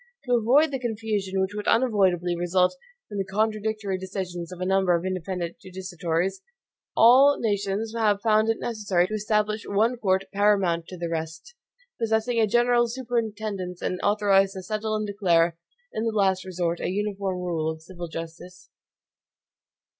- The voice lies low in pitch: No, high, 195 Hz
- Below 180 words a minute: Yes, average, 155 wpm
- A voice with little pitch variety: No, average, 3.2 semitones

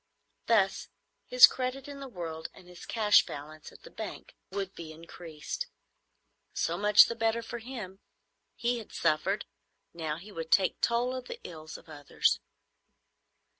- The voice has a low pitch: No, high, 195 Hz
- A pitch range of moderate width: No, wide, 6.3 semitones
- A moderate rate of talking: Yes, average, 155 wpm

